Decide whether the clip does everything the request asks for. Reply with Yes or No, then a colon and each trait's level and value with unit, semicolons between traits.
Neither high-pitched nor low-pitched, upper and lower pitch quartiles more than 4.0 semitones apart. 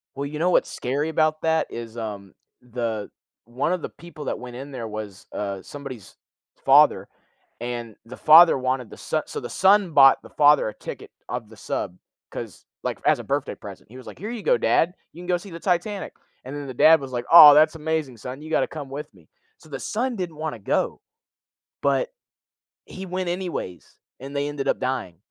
Yes: medium, 145 Hz; average, 5.2 semitones